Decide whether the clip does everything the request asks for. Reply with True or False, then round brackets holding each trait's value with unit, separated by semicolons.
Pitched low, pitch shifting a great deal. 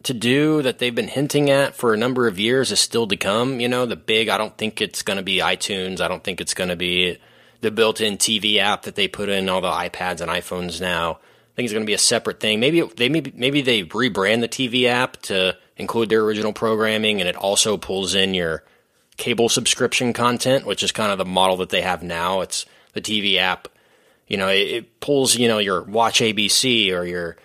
False (110 Hz; 4.6 semitones)